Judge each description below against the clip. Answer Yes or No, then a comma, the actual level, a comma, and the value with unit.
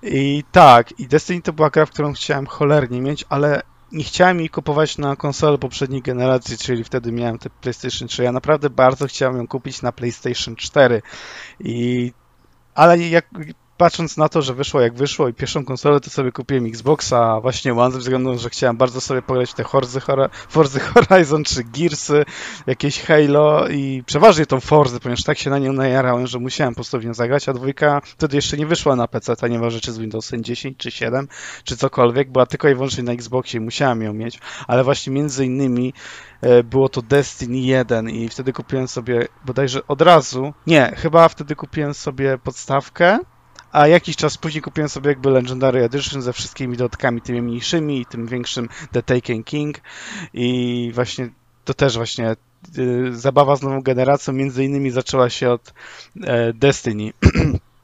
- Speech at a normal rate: No, fast, 180 wpm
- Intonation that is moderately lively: Yes, average, 3.0 semitones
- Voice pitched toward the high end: No, low, 135 Hz